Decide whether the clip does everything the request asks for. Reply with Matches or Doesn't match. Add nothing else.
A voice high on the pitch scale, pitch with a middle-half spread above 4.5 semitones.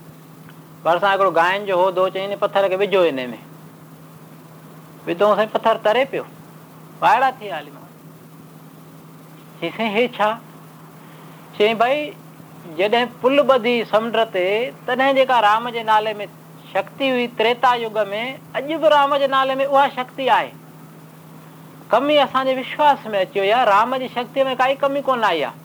Matches